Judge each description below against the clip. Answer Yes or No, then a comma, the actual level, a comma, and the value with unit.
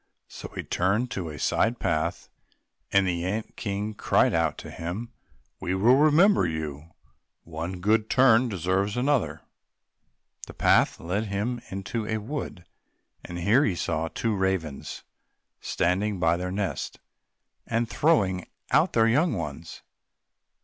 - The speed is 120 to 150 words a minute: Yes, average, 140 wpm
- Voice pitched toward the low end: Yes, low, 100 Hz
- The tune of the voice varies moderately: Yes, average, 4.7 semitones